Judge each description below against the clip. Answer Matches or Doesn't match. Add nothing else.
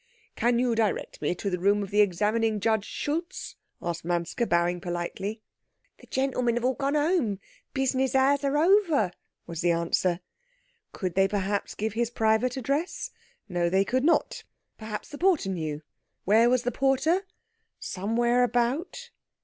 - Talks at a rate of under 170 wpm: Matches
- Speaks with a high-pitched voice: Matches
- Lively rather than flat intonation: Matches